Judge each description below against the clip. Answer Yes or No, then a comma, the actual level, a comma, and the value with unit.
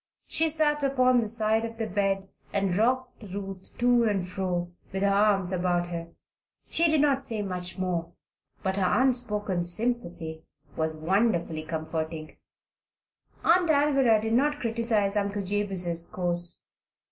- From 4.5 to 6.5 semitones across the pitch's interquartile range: Yes, average, 5.2 semitones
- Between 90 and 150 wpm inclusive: Yes, average, 140 wpm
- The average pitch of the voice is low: No, high, 200 Hz